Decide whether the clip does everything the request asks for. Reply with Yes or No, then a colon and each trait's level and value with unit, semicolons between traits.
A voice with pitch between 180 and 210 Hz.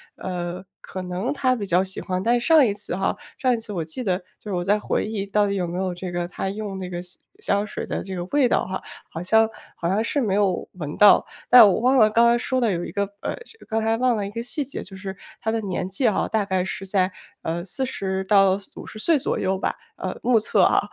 Yes: high, 200 Hz